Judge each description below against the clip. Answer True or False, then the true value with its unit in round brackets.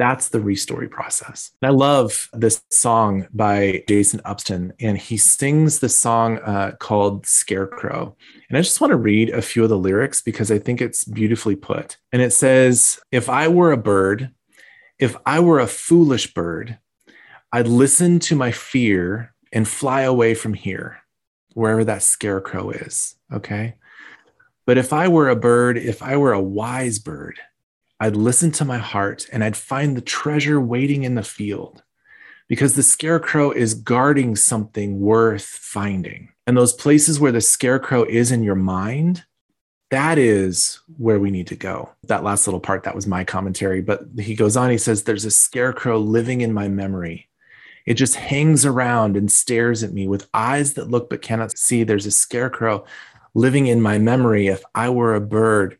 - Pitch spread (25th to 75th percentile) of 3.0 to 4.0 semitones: True (3.7 semitones)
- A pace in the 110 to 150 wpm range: False (175 wpm)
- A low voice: True (115 Hz)